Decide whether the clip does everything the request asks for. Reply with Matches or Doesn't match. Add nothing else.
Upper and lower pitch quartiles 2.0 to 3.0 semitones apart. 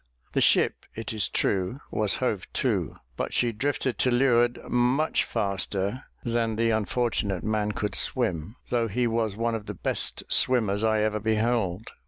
Matches